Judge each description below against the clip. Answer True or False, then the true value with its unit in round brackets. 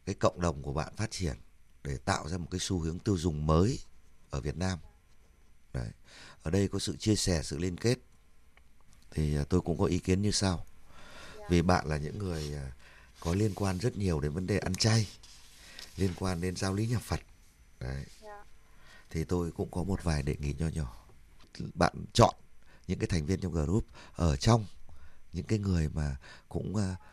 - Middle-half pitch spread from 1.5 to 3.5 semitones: False (4.3 semitones)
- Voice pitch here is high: False (85 Hz)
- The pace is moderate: True (190 wpm)